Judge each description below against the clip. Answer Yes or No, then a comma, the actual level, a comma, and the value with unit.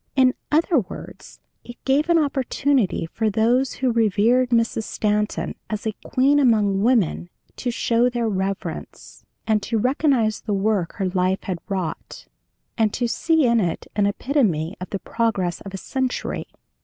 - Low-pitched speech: No, high, 225 Hz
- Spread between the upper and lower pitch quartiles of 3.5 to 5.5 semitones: Yes, average, 4.5 semitones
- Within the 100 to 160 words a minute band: Yes, average, 155 wpm